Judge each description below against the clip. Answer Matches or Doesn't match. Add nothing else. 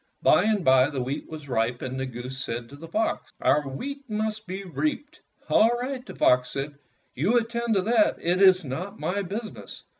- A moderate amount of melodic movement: Doesn't match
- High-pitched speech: Doesn't match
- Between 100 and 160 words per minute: Doesn't match